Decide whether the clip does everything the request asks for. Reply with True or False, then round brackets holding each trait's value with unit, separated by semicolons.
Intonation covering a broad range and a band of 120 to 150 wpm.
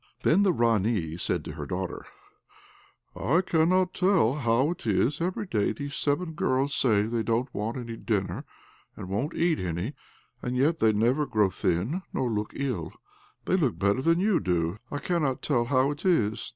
False (6.9 semitones; 180 wpm)